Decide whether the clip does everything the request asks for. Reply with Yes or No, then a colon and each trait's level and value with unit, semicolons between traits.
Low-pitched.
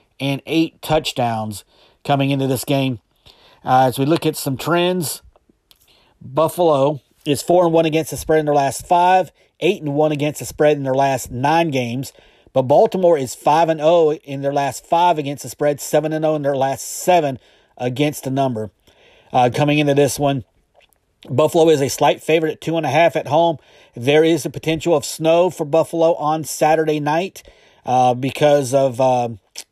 No: medium, 145 Hz